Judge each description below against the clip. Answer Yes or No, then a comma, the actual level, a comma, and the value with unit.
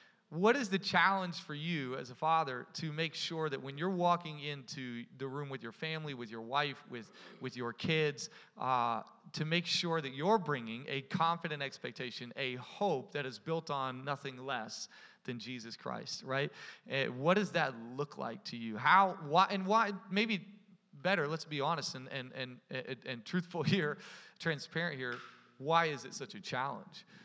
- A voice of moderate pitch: Yes, medium, 150 Hz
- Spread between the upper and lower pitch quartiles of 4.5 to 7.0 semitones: Yes, average, 4.8 semitones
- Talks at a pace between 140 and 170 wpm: No, average, 180 wpm